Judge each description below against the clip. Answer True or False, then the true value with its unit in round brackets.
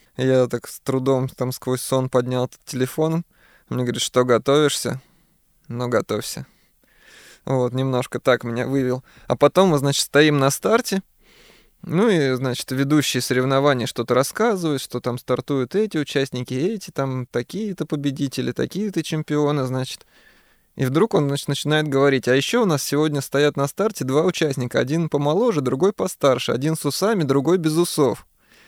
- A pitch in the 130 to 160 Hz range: True (140 Hz)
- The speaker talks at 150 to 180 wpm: True (155 wpm)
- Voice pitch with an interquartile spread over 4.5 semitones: False (3.5 semitones)